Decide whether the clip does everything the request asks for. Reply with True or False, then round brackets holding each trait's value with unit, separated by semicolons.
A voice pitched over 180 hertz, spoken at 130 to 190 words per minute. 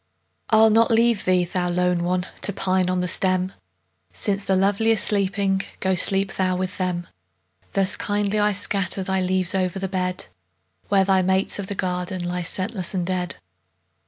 True (190 Hz; 175 wpm)